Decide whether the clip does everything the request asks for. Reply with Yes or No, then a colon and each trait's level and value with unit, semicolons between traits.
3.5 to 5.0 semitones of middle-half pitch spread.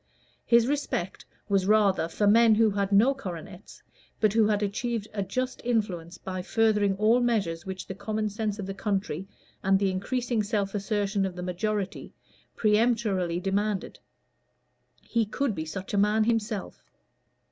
No: narrow, 2.5 semitones